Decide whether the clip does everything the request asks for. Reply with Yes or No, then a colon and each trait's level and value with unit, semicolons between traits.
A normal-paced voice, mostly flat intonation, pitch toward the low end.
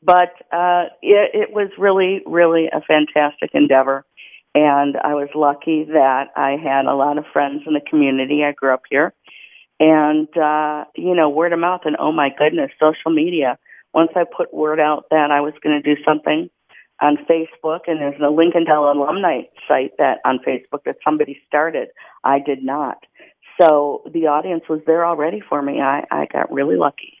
No: average, 185 wpm; narrow, 2.2 semitones; medium, 150 Hz